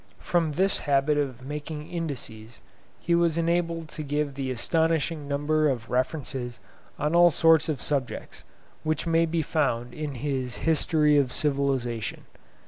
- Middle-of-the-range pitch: Yes, medium, 150 Hz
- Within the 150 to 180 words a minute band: No, average, 140 wpm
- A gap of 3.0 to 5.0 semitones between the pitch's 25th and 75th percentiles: Yes, average, 3.5 semitones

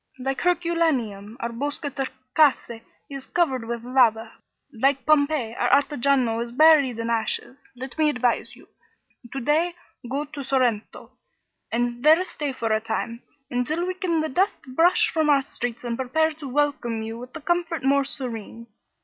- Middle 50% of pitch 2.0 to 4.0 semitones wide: No, average, 4.6 semitones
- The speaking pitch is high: Yes, very high, 270 Hz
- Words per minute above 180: No, average, 160 wpm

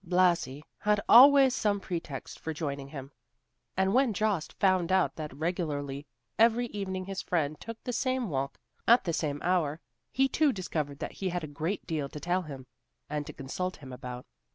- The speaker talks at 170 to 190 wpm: Yes, average, 180 wpm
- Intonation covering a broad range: Yes, wide, 5.7 semitones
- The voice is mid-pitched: Yes, medium, 175 Hz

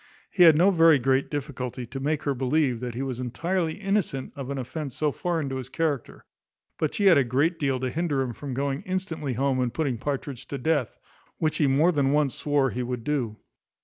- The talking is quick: Yes, fast, 215 wpm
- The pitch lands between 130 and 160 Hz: Yes, medium, 140 Hz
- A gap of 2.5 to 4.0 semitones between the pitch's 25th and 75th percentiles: Yes, average, 3.5 semitones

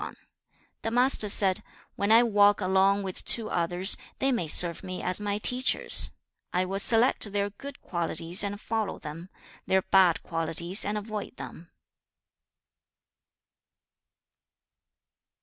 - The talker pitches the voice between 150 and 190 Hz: No, high, 200 Hz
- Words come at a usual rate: No, slow, 130 wpm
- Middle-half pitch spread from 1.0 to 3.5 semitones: Yes, average, 3.0 semitones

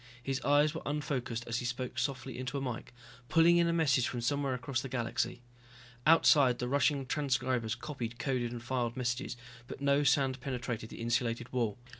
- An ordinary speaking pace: Yes, average, 180 wpm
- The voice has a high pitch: No, low, 130 Hz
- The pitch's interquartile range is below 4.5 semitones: Yes, average, 2.7 semitones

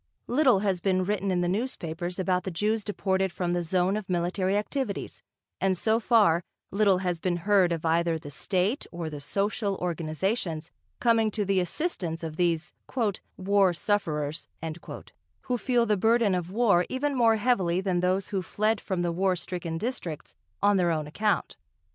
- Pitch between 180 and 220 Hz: Yes, high, 190 Hz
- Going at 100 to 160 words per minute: No, average, 170 wpm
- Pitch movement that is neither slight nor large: Yes, average, 3.4 semitones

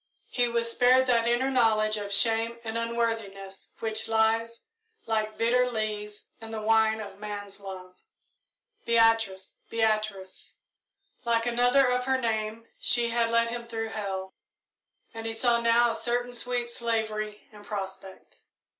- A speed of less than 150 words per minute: Yes, average, 140 wpm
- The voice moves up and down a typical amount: No, narrow, 1.6 semitones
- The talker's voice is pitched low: No, high, 225 Hz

